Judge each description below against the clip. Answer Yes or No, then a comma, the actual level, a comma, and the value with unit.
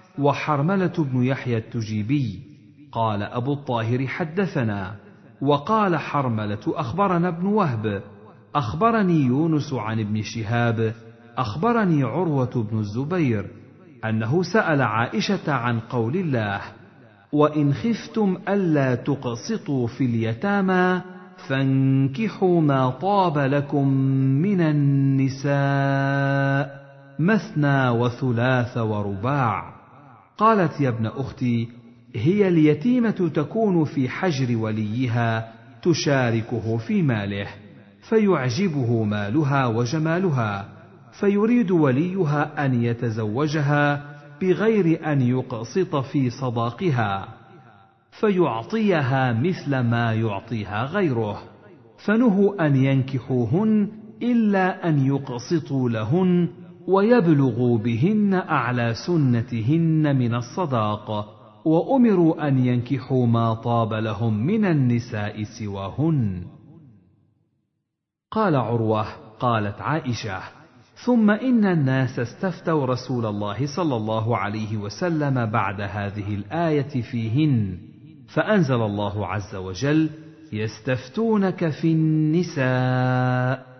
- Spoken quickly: No, average, 85 wpm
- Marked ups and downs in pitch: Yes, wide, 6.1 semitones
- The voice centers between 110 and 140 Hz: Yes, low, 135 Hz